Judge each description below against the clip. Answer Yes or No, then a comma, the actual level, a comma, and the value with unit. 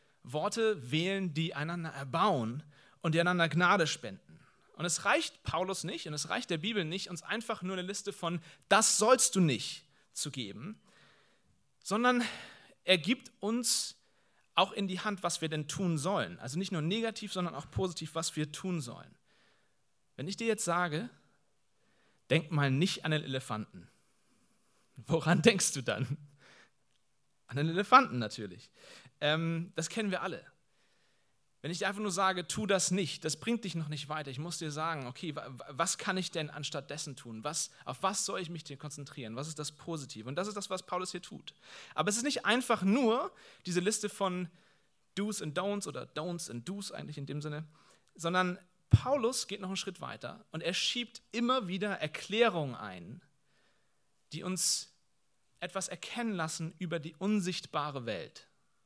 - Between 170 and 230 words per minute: Yes, average, 175 wpm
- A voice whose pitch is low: No, medium, 175 Hz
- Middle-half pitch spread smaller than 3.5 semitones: No, average, 4.8 semitones